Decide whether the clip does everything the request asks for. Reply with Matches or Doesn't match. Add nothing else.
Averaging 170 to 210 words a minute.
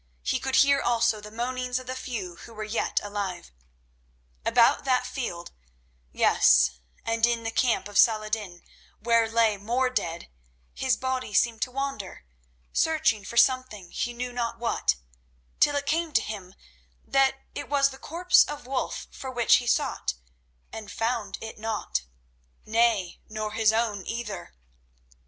Doesn't match